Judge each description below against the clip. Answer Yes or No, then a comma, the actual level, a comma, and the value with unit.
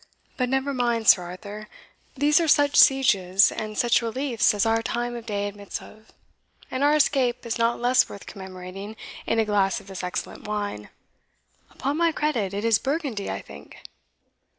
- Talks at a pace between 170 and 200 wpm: Yes, average, 175 wpm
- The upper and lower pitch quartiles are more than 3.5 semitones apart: Yes, average, 4.3 semitones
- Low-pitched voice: No, high, 225 Hz